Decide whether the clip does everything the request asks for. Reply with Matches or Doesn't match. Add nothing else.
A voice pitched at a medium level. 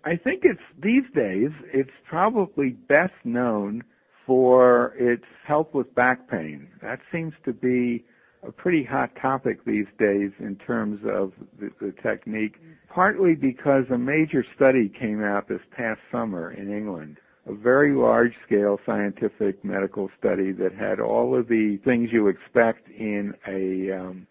Doesn't match